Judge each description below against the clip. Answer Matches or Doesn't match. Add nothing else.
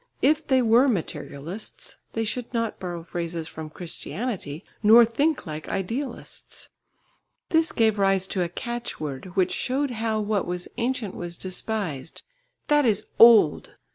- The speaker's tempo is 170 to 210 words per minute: Doesn't match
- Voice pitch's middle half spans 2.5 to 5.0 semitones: Doesn't match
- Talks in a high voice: Matches